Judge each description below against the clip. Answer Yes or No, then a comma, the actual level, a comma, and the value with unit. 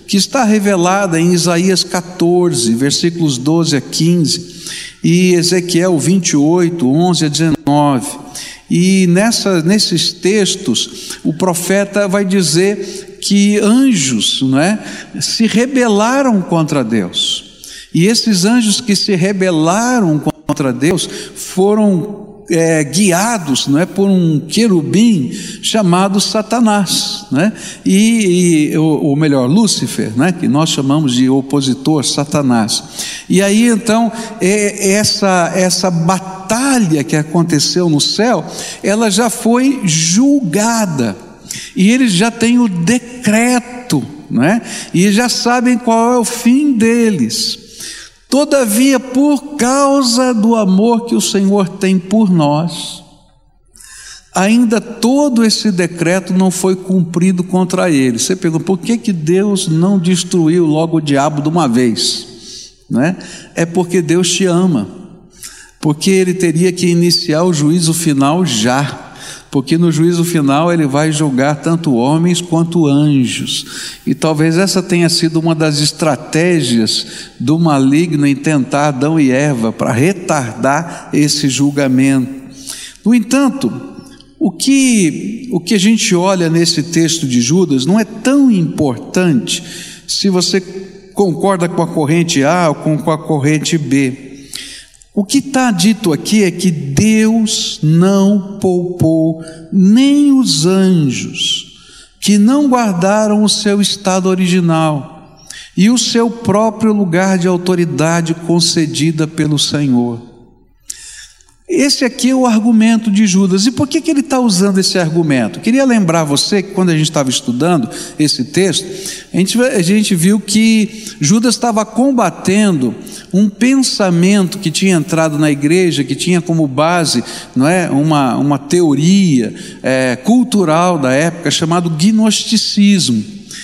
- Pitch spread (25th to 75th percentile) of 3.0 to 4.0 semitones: No, average, 5.2 semitones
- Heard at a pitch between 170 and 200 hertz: Yes, medium, 185 Hz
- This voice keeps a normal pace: Yes, average, 130 wpm